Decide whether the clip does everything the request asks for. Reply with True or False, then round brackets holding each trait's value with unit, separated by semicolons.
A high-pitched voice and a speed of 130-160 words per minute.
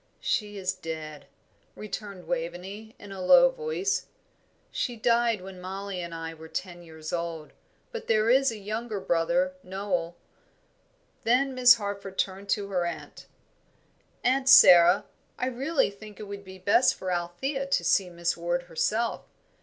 True (200 Hz; 150 wpm)